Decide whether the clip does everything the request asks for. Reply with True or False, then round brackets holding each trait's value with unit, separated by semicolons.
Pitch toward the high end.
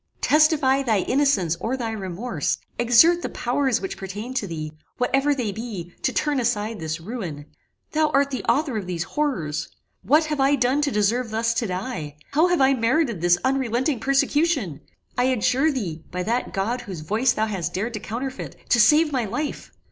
True (240 Hz)